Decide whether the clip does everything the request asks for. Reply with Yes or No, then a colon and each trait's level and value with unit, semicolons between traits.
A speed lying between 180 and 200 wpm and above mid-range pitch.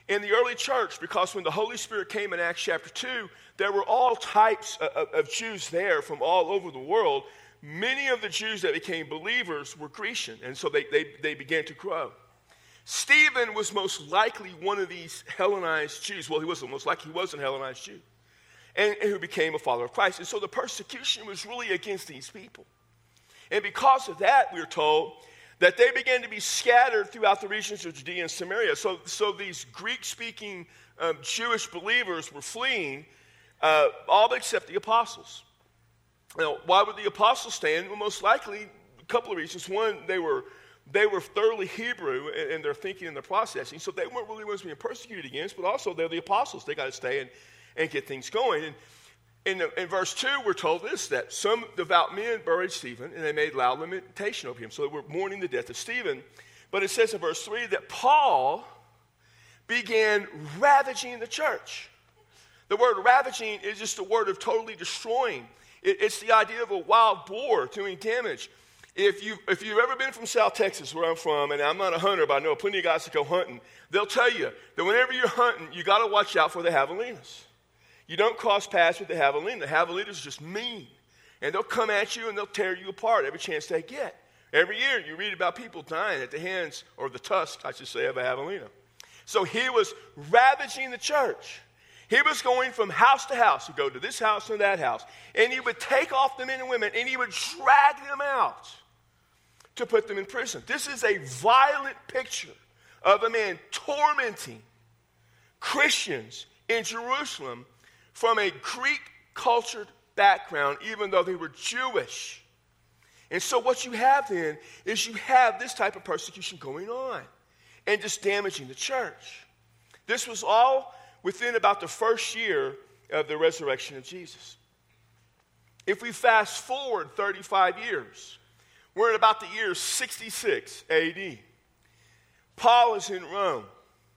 Yes: average, 190 wpm; high, 235 Hz